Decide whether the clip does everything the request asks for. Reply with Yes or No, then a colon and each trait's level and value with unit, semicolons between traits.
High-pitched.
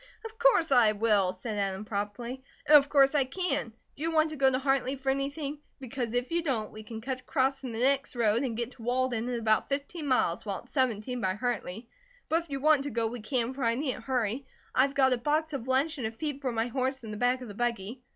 Yes: very high, 255 Hz